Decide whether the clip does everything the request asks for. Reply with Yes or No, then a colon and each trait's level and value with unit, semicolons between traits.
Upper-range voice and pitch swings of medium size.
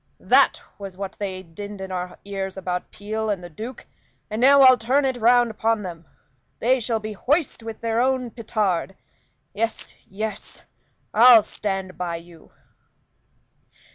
Yes: high, 215 Hz; average, 3.6 semitones